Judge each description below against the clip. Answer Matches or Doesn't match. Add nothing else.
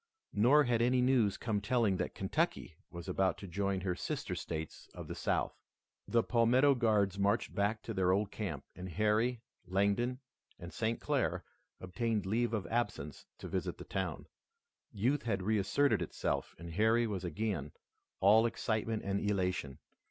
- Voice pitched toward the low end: Matches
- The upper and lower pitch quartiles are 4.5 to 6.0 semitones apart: Doesn't match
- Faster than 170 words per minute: Doesn't match